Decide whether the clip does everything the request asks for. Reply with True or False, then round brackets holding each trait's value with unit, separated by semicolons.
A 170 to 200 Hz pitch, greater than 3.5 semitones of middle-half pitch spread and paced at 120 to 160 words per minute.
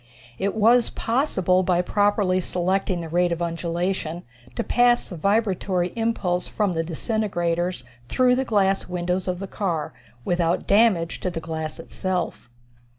False (185 Hz; 3.0 semitones; 145 wpm)